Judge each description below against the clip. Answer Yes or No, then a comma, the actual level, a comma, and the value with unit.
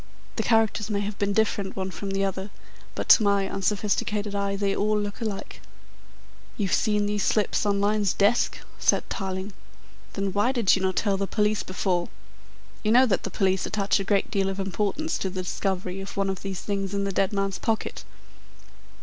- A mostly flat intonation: Yes, narrow, 1.4 semitones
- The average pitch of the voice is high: Yes, high, 200 Hz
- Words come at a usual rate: Yes, average, 190 wpm